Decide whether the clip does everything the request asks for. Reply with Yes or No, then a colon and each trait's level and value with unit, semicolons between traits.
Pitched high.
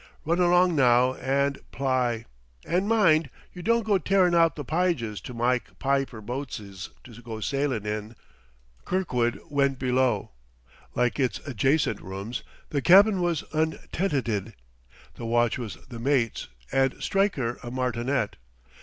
No: low, 130 Hz